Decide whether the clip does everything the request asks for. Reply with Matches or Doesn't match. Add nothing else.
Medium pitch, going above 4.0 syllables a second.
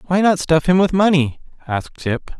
Matches